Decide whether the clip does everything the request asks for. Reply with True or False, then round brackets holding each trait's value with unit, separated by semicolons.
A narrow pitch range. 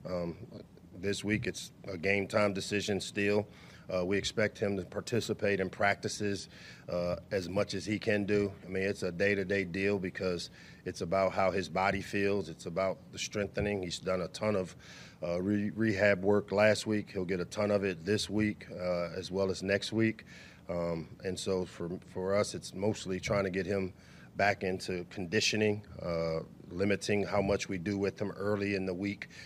True (1.8 semitones)